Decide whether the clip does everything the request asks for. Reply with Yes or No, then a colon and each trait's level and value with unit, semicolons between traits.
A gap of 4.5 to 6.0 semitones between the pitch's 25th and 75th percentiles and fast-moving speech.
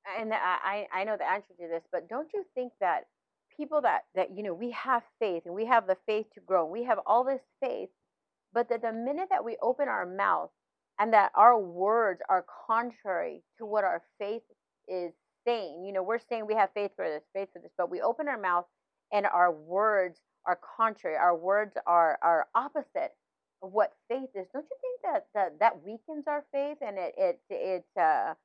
Yes: average, 5.2 semitones; fast, 210 wpm